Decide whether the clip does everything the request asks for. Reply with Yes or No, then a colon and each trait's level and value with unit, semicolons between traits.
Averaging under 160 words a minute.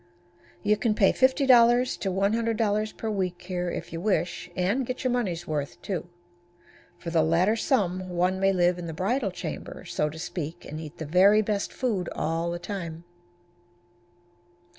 No: average, 165 wpm